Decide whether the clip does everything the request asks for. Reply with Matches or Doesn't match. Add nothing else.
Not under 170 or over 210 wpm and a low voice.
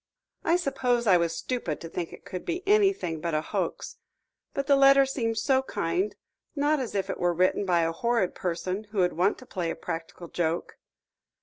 Doesn't match